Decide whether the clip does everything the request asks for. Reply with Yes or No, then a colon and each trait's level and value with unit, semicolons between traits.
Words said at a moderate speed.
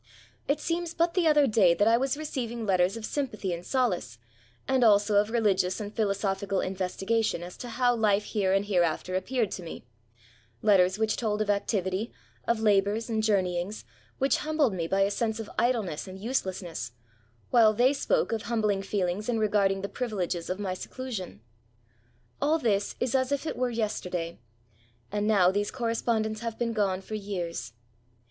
Yes: average, 170 wpm